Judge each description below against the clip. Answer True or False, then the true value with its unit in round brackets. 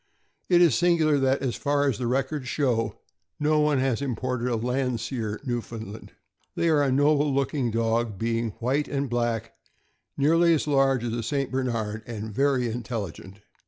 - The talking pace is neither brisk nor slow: True (170 wpm)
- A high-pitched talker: False (130 Hz)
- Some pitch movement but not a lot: True (3.7 semitones)